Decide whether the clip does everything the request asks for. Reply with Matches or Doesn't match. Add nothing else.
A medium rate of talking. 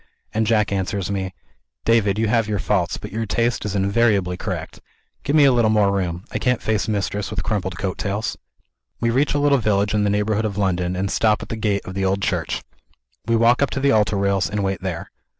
Doesn't match